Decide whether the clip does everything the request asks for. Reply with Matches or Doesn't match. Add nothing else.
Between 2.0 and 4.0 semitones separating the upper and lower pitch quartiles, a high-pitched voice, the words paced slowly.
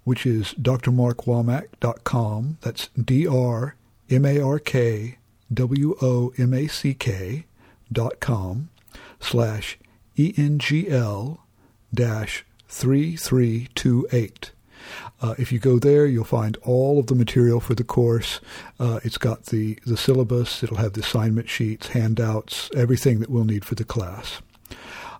Doesn't match